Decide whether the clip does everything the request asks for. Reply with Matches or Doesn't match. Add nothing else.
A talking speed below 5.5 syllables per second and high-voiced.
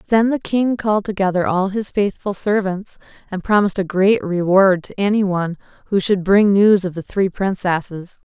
Matches